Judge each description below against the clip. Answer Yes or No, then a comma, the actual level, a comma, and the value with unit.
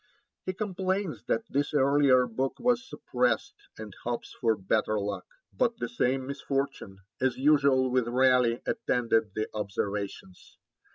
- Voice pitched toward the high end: No, low, 130 Hz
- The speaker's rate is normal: No, slow, 130 wpm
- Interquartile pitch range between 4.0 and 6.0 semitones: Yes, average, 4.5 semitones